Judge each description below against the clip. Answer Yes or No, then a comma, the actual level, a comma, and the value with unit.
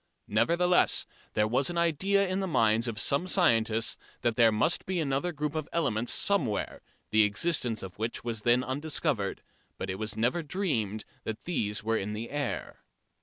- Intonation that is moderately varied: No, wide, 7.4 semitones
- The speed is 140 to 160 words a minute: No, average, 170 wpm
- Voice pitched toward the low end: Yes, low, 120 Hz